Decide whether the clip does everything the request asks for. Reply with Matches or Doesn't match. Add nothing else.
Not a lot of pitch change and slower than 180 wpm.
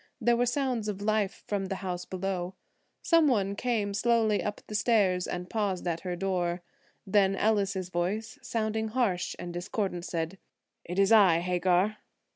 Doesn't match